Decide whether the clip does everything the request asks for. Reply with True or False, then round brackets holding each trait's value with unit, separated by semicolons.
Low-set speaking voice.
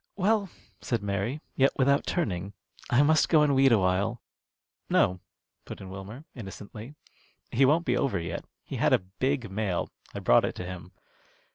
True (115 Hz)